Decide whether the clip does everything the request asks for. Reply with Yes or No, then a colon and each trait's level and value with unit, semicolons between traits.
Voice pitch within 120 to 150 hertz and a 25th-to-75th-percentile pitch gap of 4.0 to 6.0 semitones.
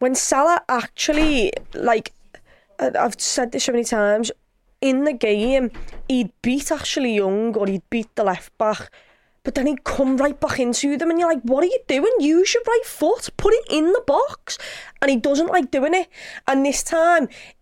No: very high, 275 Hz; wide, 5.4 semitones